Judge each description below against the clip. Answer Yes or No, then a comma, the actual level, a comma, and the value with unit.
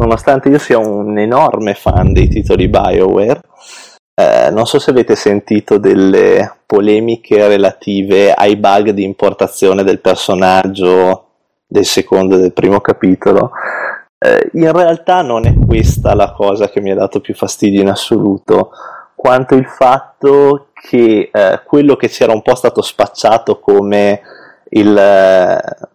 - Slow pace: No, average, 140 wpm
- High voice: No, low, 105 Hz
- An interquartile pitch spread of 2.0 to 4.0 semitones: Yes, average, 3.3 semitones